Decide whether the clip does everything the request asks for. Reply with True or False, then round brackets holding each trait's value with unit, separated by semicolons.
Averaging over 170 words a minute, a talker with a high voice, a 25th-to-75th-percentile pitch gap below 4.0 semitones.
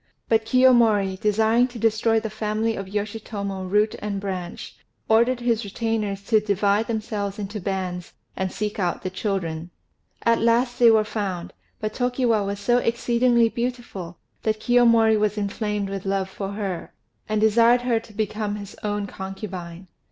False (155 wpm; 210 Hz; 2.5 semitones)